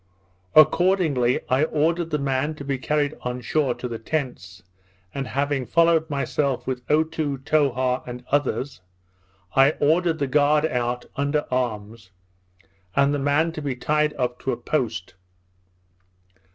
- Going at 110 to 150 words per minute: Yes, average, 140 wpm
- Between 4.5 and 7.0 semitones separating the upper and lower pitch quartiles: No, average, 3.2 semitones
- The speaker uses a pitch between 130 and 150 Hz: Yes, medium, 140 Hz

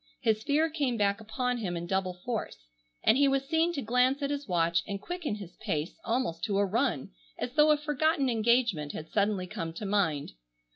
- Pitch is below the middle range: No, high, 225 Hz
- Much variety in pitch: Yes, wide, 6.5 semitones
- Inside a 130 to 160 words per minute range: No, average, 200 wpm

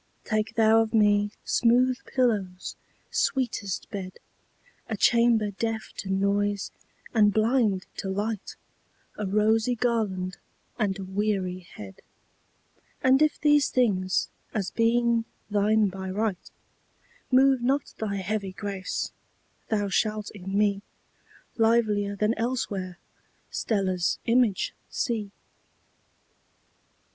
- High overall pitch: Yes, high, 210 Hz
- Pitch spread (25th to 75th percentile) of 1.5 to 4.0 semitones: Yes, average, 2.9 semitones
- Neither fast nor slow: No, slow, 95 wpm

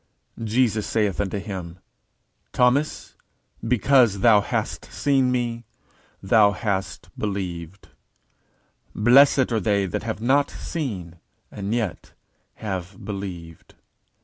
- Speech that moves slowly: Yes, slow, 100 wpm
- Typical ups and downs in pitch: Yes, average, 4.0 semitones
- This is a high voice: No, low, 105 Hz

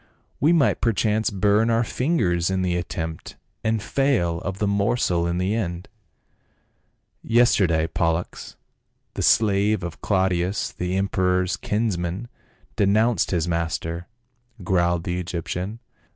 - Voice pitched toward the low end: Yes, very low, 95 Hz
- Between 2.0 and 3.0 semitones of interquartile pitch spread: No, average, 3.7 semitones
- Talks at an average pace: No, slow, 125 wpm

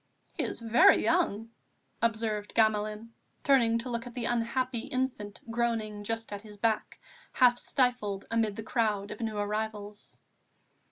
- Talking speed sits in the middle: Yes, average, 145 wpm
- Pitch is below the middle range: No, high, 225 Hz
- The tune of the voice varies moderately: No, narrow, 2.2 semitones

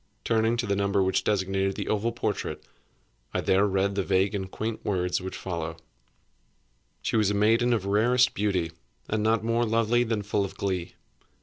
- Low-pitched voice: Yes, low, 100 Hz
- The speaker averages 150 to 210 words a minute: Yes, average, 180 wpm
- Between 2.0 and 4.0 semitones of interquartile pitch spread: Yes, average, 2.8 semitones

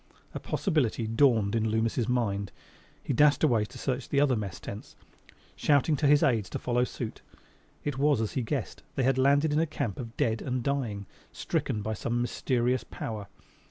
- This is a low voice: Yes, low, 120 Hz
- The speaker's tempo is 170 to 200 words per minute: Yes, average, 185 wpm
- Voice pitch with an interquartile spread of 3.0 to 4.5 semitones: Yes, average, 4.1 semitones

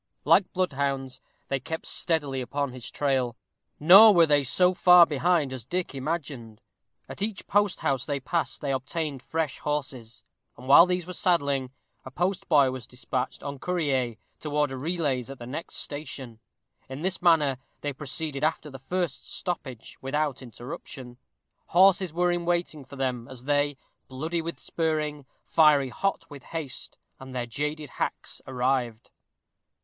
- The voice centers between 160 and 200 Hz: No, medium, 145 Hz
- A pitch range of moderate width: Yes, average, 4.2 semitones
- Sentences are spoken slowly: No, average, 155 wpm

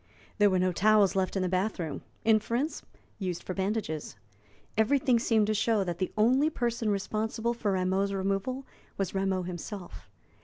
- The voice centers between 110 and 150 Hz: No, high, 200 Hz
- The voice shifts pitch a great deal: No, average, 3.1 semitones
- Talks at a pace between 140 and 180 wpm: Yes, average, 160 wpm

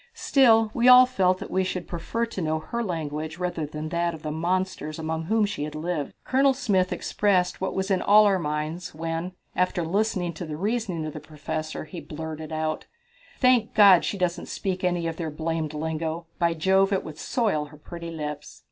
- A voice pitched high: No, medium, 170 Hz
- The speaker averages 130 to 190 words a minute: No, average, 200 wpm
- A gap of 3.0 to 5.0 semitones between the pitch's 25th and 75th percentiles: Yes, average, 3.5 semitones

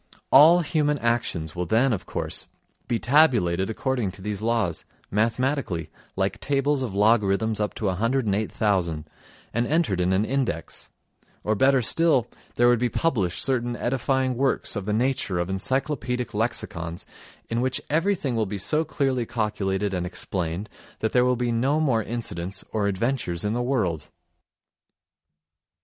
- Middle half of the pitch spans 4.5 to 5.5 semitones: Yes, average, 5.2 semitones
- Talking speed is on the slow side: No, average, 150 wpm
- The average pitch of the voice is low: Yes, low, 115 Hz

